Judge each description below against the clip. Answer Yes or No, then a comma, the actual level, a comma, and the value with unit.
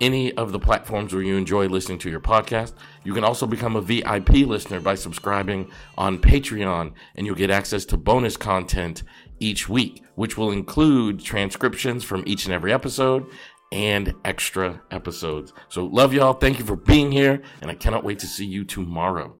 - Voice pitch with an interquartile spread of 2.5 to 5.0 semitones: Yes, average, 3.6 semitones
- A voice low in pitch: Yes, low, 100 Hz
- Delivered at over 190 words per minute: No, average, 180 wpm